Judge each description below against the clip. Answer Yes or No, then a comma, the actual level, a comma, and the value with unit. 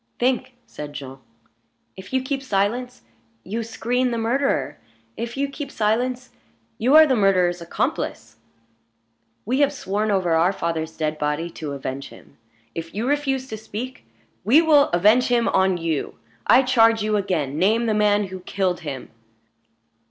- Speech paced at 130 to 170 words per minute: Yes, average, 155 wpm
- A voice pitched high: Yes, high, 215 Hz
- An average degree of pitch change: No, wide, 6.5 semitones